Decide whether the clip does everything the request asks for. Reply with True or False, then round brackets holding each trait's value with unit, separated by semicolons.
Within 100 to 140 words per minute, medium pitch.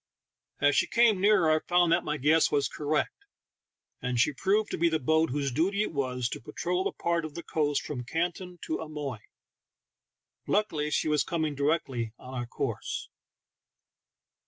False (175 wpm; 155 Hz)